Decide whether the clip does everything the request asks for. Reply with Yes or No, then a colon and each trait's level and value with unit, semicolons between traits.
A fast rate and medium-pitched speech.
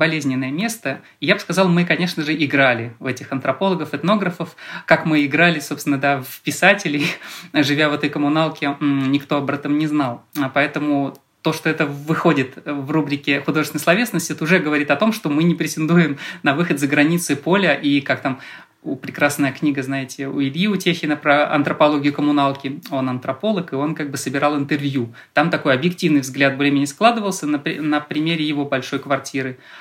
Yes: fast, 175 wpm; medium, 150 Hz